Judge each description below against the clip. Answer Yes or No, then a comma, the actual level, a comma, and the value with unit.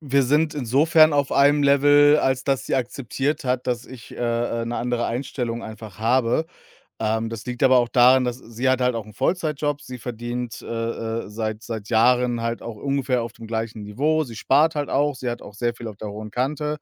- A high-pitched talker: No, low, 125 Hz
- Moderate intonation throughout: Yes, average, 3.3 semitones